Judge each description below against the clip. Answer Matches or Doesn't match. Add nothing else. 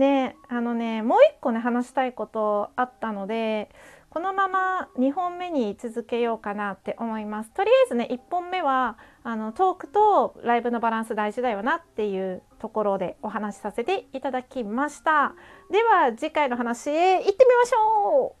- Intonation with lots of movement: Matches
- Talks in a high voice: Matches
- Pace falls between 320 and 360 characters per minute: Matches